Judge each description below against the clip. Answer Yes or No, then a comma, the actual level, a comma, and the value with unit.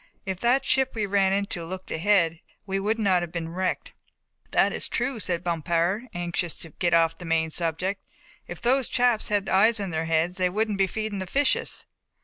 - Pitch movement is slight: No, average, 3.9 semitones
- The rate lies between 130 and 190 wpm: No, average, 200 wpm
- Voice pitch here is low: No, high, 190 Hz